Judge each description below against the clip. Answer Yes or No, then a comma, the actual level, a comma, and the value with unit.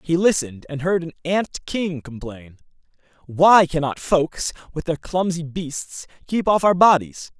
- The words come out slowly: No, average, 155 wpm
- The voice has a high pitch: No, medium, 160 Hz